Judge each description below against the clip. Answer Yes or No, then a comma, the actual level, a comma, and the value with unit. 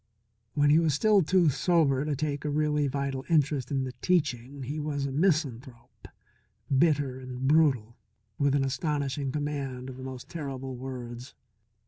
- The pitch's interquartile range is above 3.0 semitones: No, narrow, 2.5 semitones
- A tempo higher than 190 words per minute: No, average, 155 wpm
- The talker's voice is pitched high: No, medium, 140 Hz